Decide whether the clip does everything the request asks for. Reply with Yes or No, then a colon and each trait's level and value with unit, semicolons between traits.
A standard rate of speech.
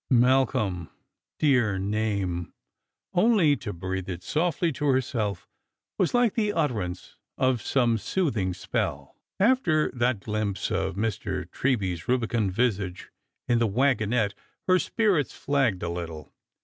No: slow, 125 wpm